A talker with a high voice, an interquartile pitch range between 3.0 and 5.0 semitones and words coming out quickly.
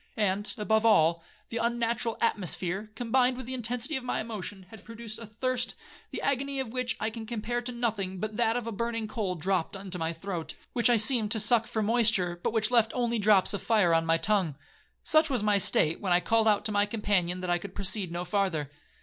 Yes: high, 215 Hz; average, 3.6 semitones; fast, 220 wpm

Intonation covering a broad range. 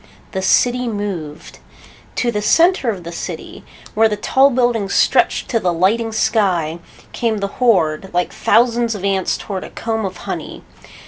No: average, 3.8 semitones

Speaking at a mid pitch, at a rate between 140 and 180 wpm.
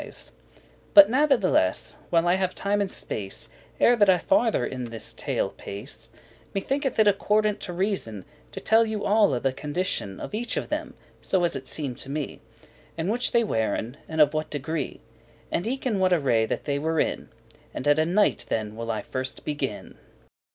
No: medium, 165 Hz; average, 190 wpm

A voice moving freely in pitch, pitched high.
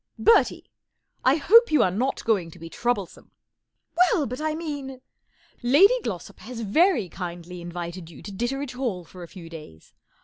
Yes: wide, 8.4 semitones; high, 230 Hz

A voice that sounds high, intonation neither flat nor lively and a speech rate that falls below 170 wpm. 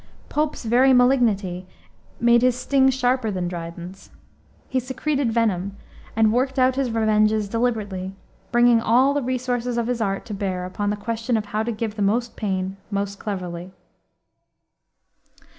Yes: high, 225 Hz; average, 3.9 semitones; average, 150 wpm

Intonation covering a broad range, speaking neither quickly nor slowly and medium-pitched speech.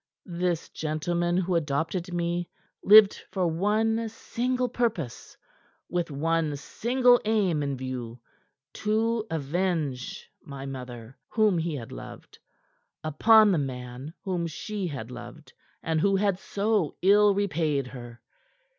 No: wide, 6.4 semitones; slow, 120 wpm; medium, 170 Hz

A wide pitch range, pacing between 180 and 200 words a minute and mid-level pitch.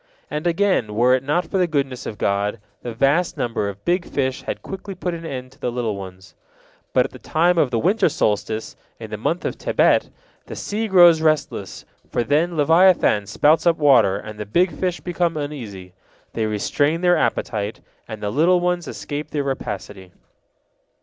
Yes: wide, 7.8 semitones; average, 185 wpm; medium, 145 Hz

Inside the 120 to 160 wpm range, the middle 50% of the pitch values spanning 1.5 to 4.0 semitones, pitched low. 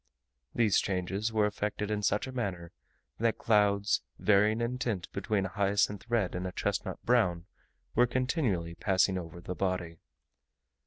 Yes: average, 150 wpm; average, 3.3 semitones; low, 100 Hz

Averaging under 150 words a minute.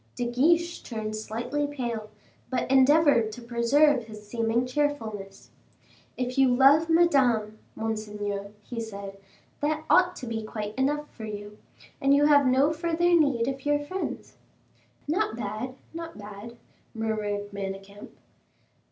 Yes: slow, 135 wpm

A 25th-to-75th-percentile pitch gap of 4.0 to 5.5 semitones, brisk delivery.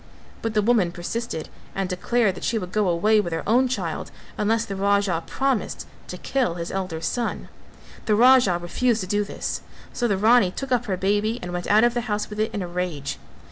Yes: average, 4.3 semitones; fast, 215 wpm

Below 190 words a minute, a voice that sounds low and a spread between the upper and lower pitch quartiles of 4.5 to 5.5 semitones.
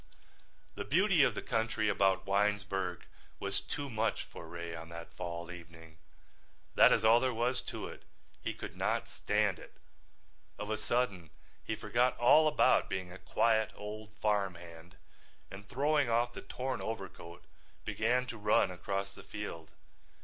Yes: average, 155 wpm; low, 105 Hz; average, 4.9 semitones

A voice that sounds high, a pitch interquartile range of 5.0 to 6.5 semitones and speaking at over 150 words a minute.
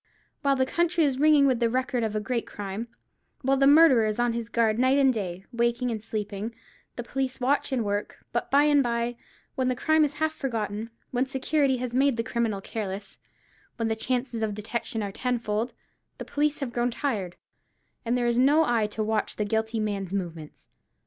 No: high, 235 Hz; average, 3.6 semitones; average, 190 wpm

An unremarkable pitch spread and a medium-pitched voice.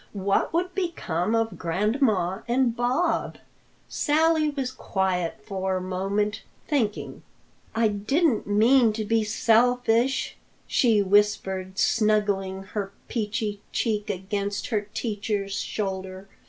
No: average, 3.6 semitones; high, 210 Hz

